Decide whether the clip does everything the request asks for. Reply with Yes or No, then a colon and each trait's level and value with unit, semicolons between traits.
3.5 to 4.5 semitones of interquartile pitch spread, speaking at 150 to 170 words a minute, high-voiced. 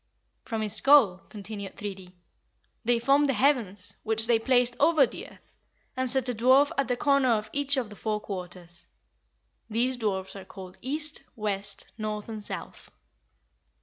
Yes: average, 4.2 semitones; average, 160 wpm; high, 225 Hz